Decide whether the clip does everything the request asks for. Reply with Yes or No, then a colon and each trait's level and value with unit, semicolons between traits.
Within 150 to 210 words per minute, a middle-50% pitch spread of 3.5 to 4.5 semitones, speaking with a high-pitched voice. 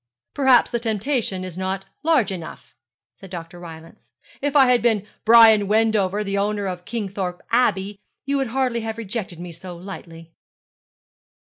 Yes: average, 155 wpm; average, 4.1 semitones; high, 205 Hz